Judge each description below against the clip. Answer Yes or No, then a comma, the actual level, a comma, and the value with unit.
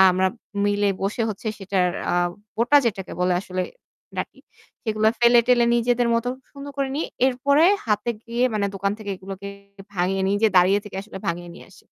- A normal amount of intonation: Yes, average, 3.8 semitones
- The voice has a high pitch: Yes, high, 210 Hz